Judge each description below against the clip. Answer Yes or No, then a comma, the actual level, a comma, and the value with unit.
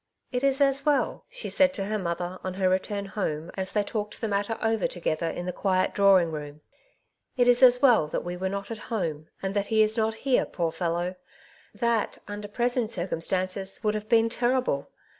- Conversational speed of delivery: No, fast, 215 wpm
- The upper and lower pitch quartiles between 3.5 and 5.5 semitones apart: Yes, average, 3.9 semitones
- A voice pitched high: Yes, high, 200 Hz